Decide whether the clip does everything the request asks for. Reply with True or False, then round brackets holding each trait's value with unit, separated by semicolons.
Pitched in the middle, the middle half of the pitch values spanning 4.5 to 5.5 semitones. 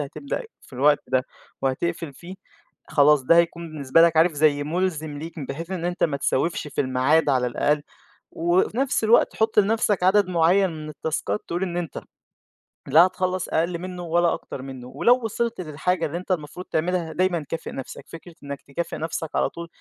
False (165 Hz; 3.6 semitones)